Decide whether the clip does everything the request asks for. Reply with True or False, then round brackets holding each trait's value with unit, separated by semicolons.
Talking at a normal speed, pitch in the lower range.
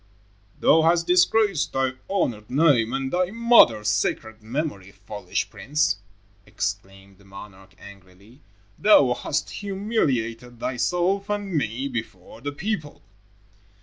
False (115 wpm; 130 Hz)